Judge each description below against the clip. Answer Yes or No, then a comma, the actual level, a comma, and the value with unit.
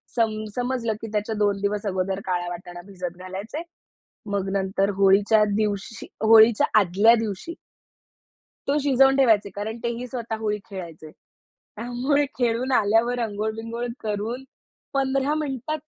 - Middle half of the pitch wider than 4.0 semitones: No, average, 3.6 semitones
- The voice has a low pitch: No, high, 220 Hz